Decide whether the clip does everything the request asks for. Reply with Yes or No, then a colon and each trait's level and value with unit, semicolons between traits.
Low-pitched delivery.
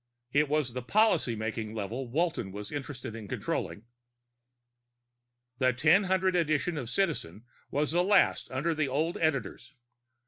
No: medium, 145 Hz